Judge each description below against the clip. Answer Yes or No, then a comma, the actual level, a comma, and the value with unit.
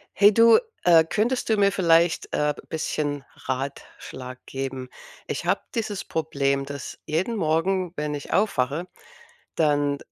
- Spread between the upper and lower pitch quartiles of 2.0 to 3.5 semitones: No, wide, 5.5 semitones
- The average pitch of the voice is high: No, medium, 160 Hz